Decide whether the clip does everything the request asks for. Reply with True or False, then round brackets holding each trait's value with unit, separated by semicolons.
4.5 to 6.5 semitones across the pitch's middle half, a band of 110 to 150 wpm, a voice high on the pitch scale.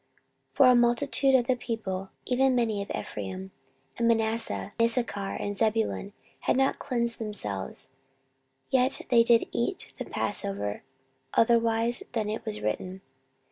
False (3.7 semitones; 140 wpm; 225 Hz)